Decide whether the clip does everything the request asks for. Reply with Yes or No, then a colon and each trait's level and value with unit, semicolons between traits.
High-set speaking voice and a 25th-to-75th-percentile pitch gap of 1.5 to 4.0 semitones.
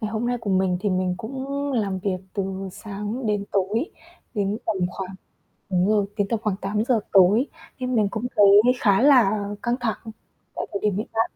Yes: high, 210 Hz; average, 2.9 semitones